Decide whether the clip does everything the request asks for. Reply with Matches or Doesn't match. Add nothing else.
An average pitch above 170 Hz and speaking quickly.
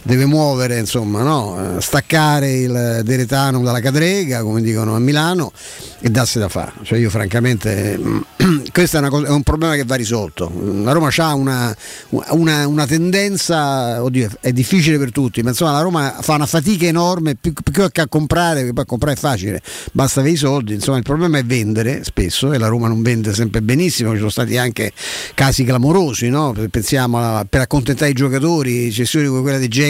Doesn't match